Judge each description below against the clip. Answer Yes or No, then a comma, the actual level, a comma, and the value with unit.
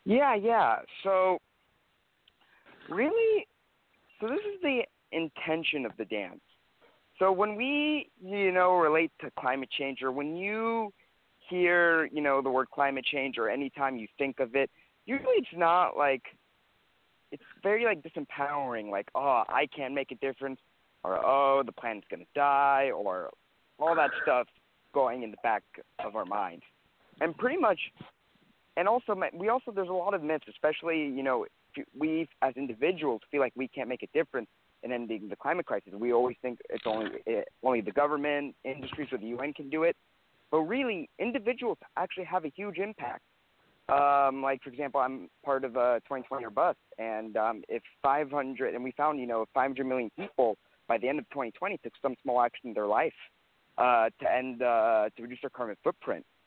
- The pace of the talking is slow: No, average, 180 wpm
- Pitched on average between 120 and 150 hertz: Yes, medium, 140 Hz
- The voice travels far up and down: Yes, wide, 5.9 semitones